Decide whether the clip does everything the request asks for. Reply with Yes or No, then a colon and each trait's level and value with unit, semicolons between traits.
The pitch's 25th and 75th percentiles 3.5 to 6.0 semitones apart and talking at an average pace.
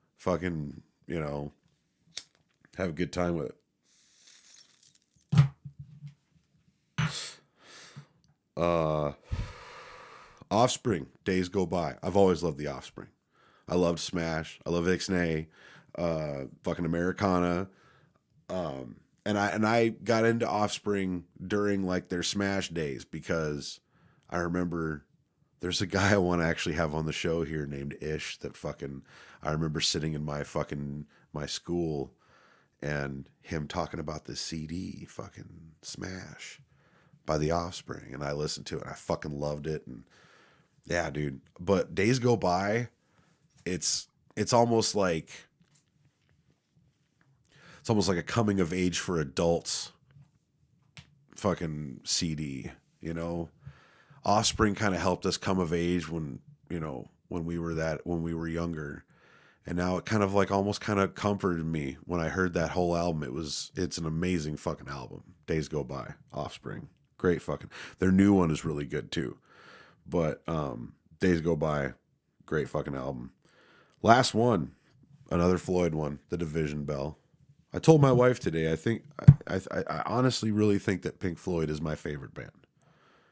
Yes: average, 4.6 semitones; average, 150 wpm